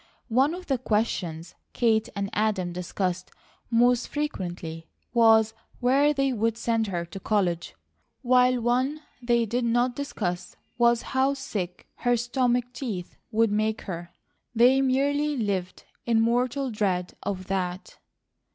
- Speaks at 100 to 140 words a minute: Yes, slow, 135 wpm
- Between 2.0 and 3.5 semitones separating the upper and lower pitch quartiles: No, average, 4.7 semitones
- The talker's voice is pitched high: Yes, high, 230 Hz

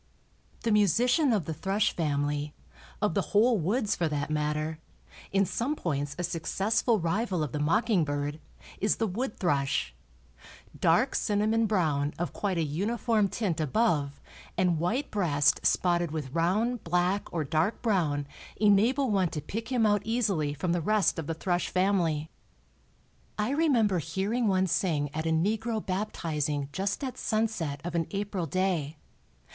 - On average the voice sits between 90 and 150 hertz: No, medium, 185 Hz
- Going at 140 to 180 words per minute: Yes, average, 155 wpm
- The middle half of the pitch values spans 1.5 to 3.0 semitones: No, wide, 5.5 semitones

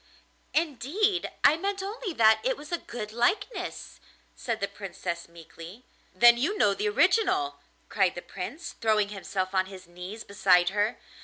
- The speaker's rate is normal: Yes, average, 155 wpm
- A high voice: Yes, high, 220 Hz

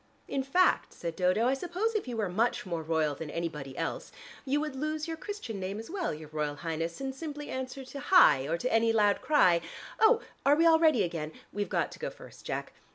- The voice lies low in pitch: No, high, 225 Hz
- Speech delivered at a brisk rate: Yes, fast, 220 wpm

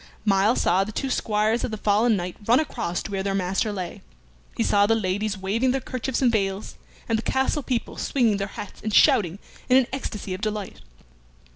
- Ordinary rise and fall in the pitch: Yes, average, 3.3 semitones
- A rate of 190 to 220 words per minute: Yes, average, 200 wpm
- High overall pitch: Yes, high, 210 Hz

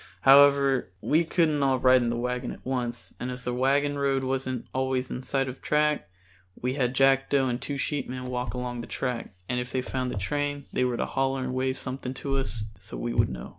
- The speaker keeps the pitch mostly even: Yes, narrow, 1.7 semitones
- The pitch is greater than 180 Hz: No, low, 130 Hz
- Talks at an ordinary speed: No, fast, 235 wpm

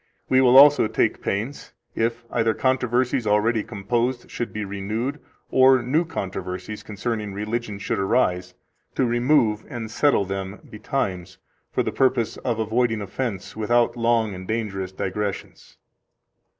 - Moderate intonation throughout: Yes, average, 3.5 semitones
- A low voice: Yes, low, 110 Hz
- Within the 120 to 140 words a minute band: Yes, slow, 135 wpm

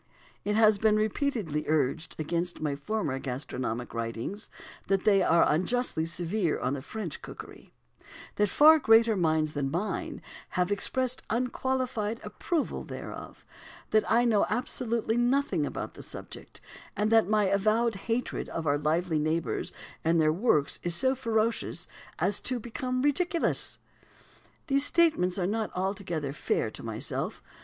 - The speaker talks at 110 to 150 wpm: Yes, average, 140 wpm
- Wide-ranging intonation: Yes, wide, 6.6 semitones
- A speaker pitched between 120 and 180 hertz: No, high, 205 Hz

